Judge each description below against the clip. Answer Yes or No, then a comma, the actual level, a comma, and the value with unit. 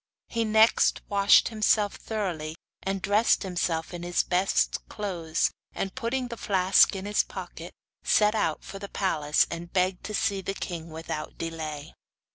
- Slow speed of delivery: No, average, 155 wpm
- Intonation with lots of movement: No, average, 3.9 semitones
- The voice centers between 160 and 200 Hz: Yes, high, 190 Hz